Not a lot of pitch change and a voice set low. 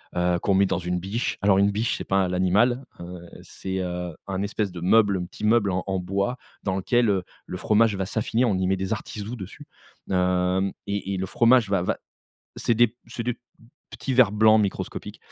No: average, 3.1 semitones; low, 100 Hz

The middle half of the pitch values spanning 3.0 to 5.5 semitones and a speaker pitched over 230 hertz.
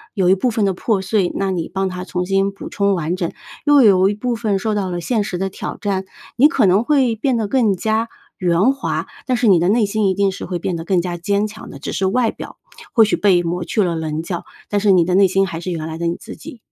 No: average, 3.3 semitones; high, 195 Hz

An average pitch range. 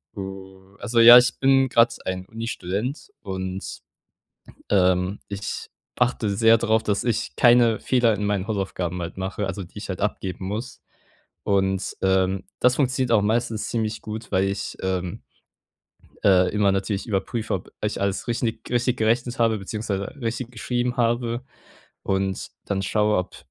Yes: average, 3.4 semitones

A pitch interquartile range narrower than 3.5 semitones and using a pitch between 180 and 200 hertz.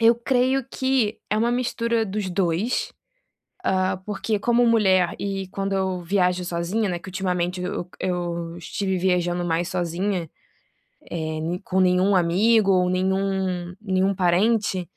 Yes: average, 2.8 semitones; high, 190 Hz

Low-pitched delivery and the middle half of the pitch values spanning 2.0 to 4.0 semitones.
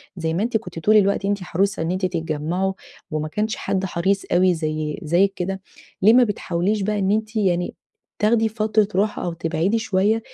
No: high, 190 Hz; average, 3.7 semitones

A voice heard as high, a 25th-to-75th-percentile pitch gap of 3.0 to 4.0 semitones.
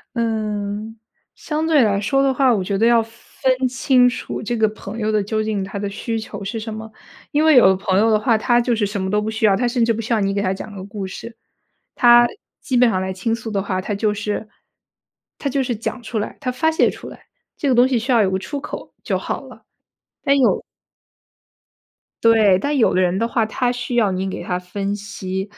Yes: high, 220 Hz; average, 3.3 semitones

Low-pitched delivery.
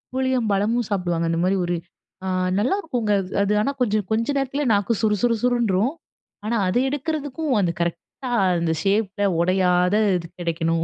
No: high, 210 Hz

